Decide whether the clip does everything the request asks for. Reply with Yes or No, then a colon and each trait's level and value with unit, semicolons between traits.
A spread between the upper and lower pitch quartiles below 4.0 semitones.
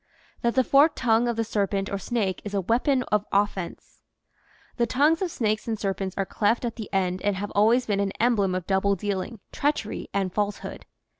Yes: average, 3.3 semitones